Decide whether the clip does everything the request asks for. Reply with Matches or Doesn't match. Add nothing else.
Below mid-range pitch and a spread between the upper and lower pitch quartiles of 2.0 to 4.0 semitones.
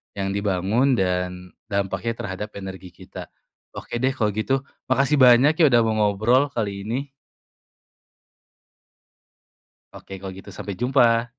Doesn't match